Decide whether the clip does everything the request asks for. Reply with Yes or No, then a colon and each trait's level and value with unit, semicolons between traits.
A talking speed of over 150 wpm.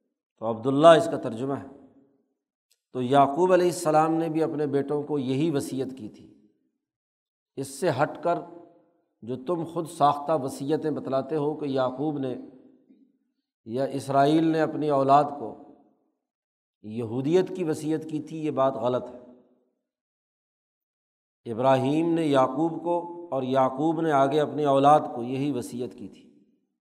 No: average, 140 wpm